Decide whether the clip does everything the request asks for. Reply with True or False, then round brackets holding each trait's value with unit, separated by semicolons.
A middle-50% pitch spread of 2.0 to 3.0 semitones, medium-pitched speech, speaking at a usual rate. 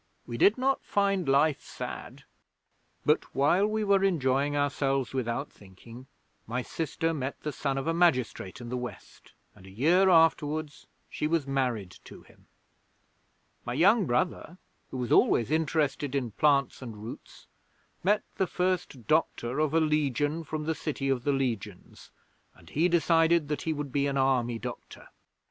False (4.2 semitones; 145 Hz; 160 wpm)